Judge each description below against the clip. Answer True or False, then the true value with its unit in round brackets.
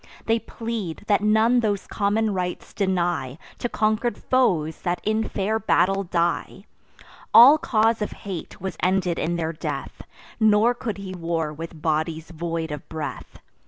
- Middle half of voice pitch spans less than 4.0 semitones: False (4.7 semitones)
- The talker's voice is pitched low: False (190 Hz)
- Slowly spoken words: False (150 wpm)